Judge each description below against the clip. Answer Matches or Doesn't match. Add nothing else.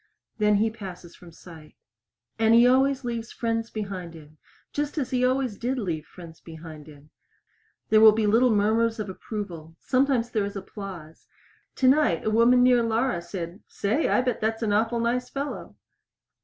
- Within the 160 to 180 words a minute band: Matches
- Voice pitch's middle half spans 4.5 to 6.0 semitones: Matches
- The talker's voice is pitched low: Doesn't match